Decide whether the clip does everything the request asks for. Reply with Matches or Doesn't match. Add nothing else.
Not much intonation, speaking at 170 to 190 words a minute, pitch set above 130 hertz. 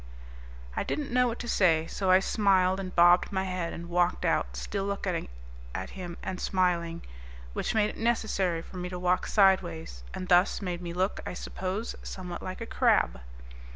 Matches